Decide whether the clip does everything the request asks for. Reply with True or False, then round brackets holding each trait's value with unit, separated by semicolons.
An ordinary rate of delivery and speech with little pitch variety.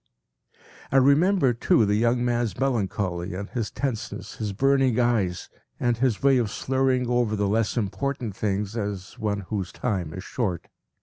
False (165 wpm; 4.0 semitones)